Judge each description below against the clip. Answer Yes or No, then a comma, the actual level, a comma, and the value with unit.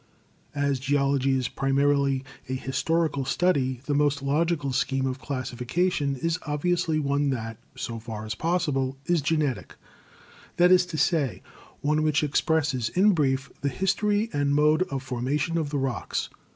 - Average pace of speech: Yes, average, 150 wpm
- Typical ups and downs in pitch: Yes, average, 3.3 semitones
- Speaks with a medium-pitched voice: Yes, medium, 145 Hz